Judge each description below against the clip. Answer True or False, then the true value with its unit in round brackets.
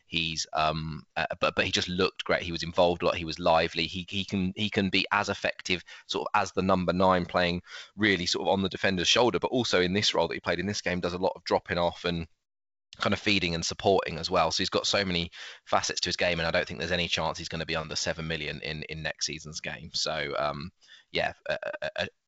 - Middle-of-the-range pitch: False (90 Hz)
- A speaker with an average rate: False (265 wpm)